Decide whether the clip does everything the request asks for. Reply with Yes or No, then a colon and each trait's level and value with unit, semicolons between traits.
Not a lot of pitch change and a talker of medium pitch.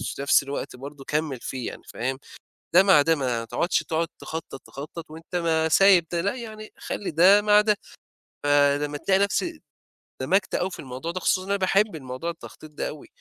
No: average, 5.2 semitones; medium, 165 Hz